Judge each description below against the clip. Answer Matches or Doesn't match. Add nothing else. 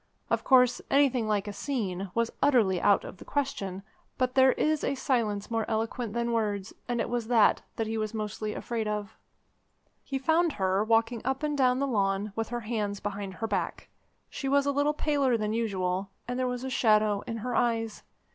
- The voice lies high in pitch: Matches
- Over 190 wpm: Matches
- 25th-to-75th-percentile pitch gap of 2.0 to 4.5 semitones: Matches